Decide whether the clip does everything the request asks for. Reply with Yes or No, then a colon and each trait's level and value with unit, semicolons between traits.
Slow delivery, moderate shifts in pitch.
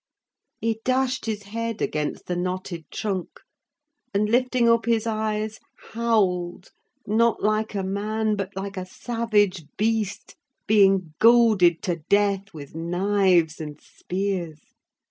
Yes: slow, 125 wpm; average, 3.3 semitones